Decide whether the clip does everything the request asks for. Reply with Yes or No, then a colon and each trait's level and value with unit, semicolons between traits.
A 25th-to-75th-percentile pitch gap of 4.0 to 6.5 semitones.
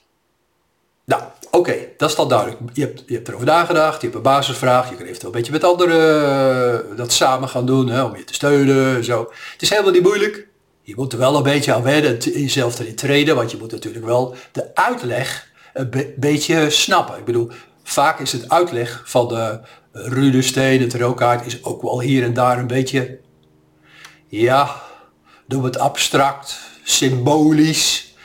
No: average, 3.0 semitones